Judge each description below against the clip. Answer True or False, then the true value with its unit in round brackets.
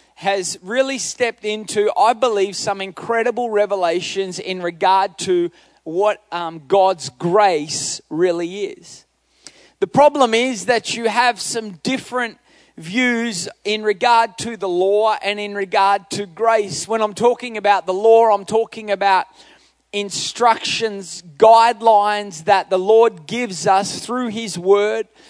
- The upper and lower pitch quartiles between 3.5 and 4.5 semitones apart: False (3.1 semitones)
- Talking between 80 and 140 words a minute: True (135 wpm)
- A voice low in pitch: False (210 Hz)